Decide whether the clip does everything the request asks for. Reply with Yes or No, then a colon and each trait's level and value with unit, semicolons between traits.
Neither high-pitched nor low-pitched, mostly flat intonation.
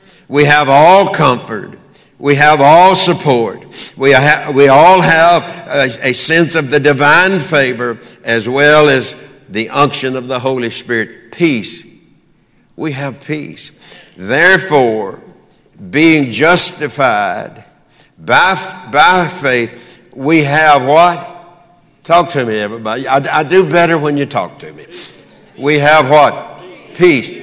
No: medium, 145 Hz; average, 4.2 semitones